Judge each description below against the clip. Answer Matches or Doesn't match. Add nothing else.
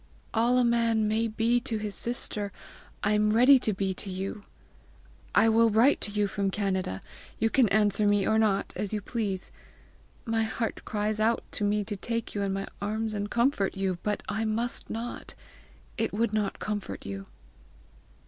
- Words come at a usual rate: Matches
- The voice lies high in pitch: Matches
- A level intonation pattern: Matches